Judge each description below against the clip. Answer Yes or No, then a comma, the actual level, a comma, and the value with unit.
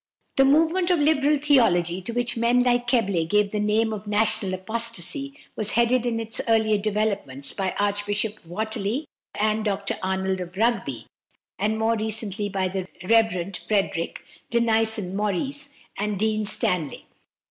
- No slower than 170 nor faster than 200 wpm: No, average, 145 wpm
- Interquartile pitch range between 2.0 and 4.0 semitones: Yes, average, 3.1 semitones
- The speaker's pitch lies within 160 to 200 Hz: No, high, 215 Hz